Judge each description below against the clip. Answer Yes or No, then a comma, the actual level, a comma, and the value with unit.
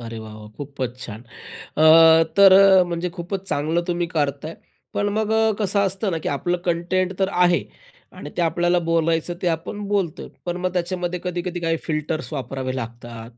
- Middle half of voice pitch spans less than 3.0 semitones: No, average, 3.9 semitones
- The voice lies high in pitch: No, medium, 170 Hz